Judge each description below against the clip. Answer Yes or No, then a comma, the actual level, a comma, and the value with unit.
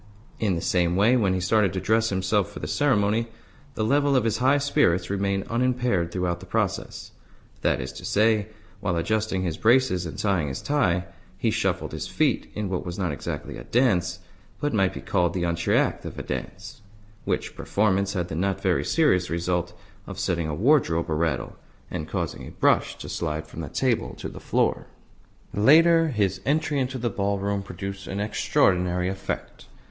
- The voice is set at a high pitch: No, low, 100 Hz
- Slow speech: No, average, 185 wpm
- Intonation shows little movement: No, average, 4.2 semitones